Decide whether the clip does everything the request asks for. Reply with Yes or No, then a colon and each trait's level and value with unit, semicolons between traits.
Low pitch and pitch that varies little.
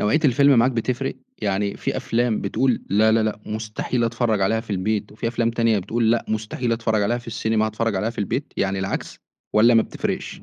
Yes: low, 110 Hz; narrow, 1.8 semitones